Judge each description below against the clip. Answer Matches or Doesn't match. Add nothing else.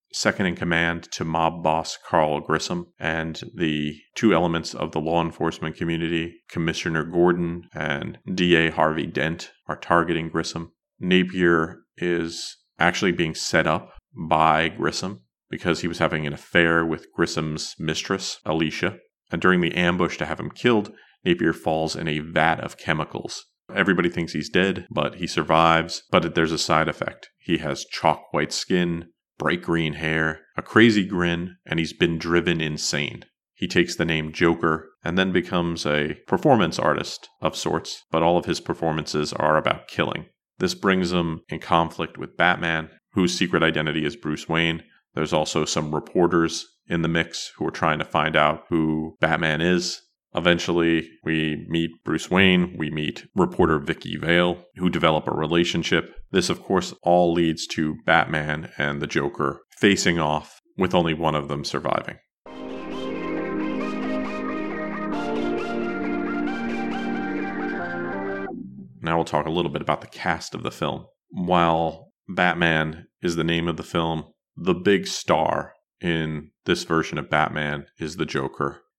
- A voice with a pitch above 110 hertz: Doesn't match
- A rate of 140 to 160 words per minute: Matches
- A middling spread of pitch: Doesn't match